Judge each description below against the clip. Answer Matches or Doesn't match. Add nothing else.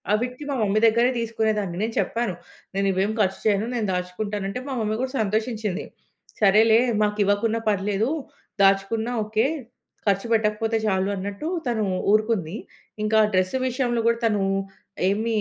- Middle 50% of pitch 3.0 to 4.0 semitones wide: Doesn't match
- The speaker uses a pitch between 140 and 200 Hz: Doesn't match